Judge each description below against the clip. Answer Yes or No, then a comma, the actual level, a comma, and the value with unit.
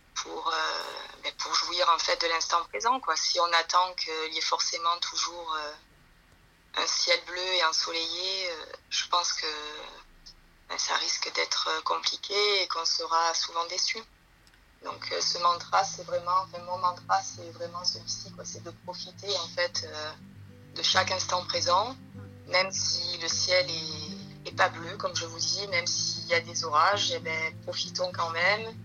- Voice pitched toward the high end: No, medium, 170 Hz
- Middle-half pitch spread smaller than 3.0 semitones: Yes, narrow, 2.4 semitones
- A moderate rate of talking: Yes, average, 175 wpm